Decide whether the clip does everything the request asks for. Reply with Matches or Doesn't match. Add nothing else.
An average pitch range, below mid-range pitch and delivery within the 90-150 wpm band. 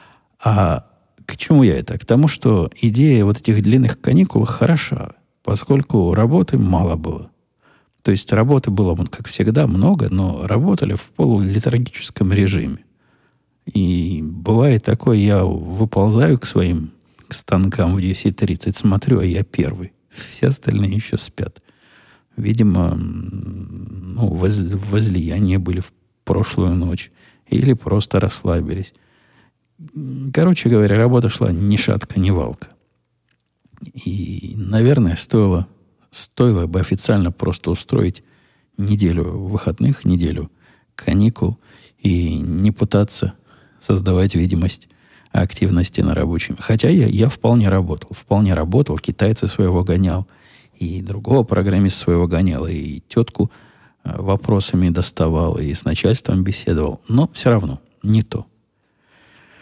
Matches